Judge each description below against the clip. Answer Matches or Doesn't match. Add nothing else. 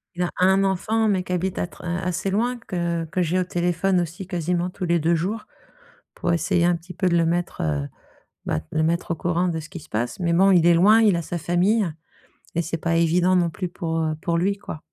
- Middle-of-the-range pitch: Matches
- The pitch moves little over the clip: Matches